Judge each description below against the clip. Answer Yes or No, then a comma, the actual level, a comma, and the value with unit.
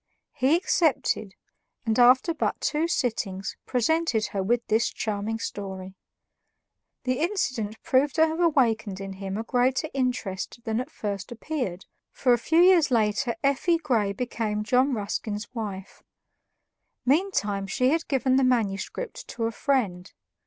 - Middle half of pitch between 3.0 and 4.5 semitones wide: No, average, 5.1 semitones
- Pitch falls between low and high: No, high, 240 Hz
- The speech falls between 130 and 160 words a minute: Yes, average, 140 wpm